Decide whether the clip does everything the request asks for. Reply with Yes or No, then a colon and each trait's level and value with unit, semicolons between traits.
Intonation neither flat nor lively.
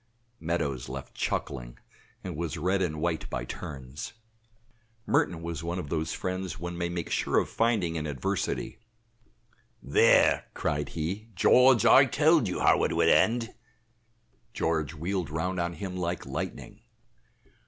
Yes: average, 3.2 semitones